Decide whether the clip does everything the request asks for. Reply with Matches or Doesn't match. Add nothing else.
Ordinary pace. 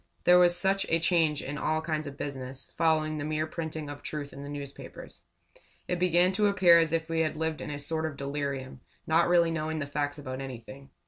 Doesn't match